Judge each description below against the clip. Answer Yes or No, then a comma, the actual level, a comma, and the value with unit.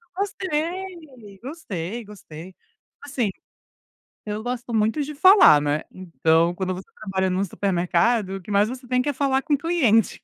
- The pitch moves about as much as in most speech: No, wide, 7.2 semitones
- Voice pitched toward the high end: Yes, high, 220 Hz